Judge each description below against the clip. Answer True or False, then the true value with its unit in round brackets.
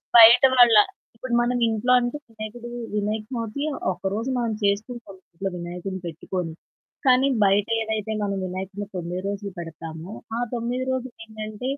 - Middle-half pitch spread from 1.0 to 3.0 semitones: False (3.7 semitones)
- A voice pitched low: False (215 Hz)